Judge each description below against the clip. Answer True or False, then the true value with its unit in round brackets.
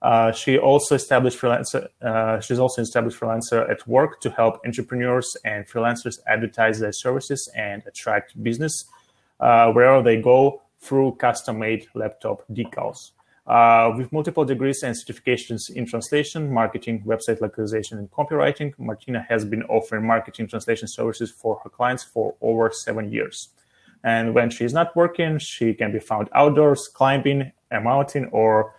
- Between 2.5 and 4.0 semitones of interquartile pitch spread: True (3.1 semitones)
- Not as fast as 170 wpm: True (150 wpm)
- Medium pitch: False (120 Hz)